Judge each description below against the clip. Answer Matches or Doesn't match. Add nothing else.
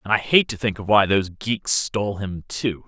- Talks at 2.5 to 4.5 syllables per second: Doesn't match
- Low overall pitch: Matches